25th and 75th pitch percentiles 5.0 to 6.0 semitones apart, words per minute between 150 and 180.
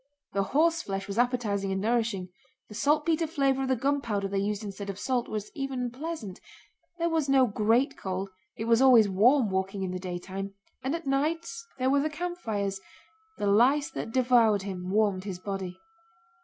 Yes: wide, 5.6 semitones; average, 175 wpm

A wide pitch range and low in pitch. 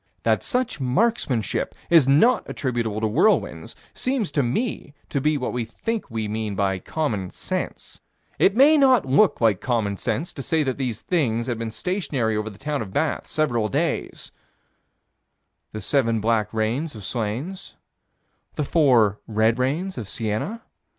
Yes: wide, 6.6 semitones; low, 125 Hz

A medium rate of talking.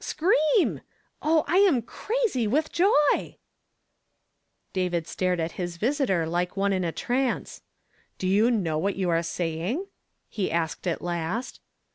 Yes: average, 145 wpm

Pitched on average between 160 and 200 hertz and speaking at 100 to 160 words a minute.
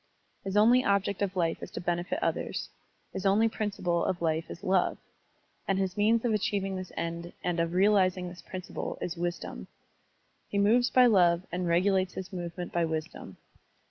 No: medium, 185 Hz; average, 175 wpm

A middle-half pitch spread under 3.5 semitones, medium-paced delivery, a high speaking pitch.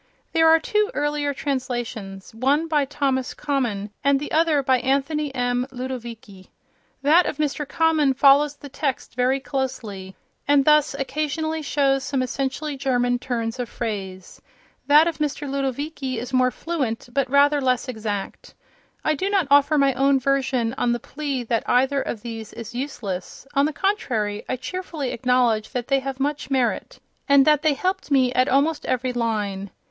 Yes: average, 3.0 semitones; average, 165 wpm; very high, 270 Hz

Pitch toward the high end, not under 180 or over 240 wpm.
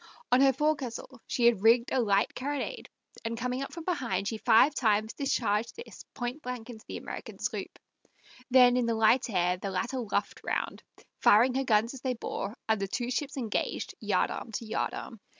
Yes: high, 240 Hz; average, 190 wpm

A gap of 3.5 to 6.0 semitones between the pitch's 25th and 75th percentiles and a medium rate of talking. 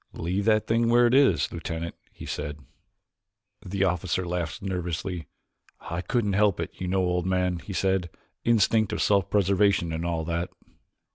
No: average, 3.0 semitones; average, 160 wpm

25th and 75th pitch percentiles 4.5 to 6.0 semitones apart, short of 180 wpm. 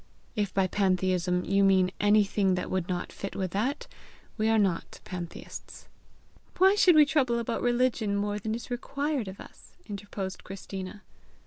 No: average, 3.9 semitones; average, 155 wpm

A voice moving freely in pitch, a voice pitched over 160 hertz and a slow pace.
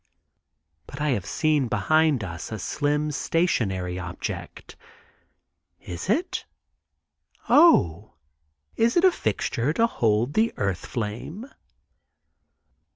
No: wide, 8.4 semitones; low, 135 Hz; slow, 100 wpm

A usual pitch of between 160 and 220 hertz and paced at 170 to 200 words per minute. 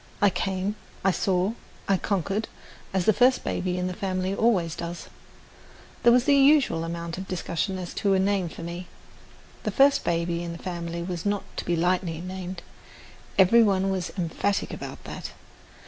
Yes: medium, 185 Hz; average, 175 wpm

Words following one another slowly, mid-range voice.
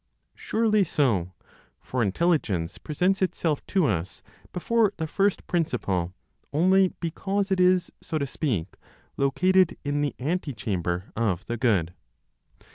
Yes: slow, 120 wpm; medium, 150 Hz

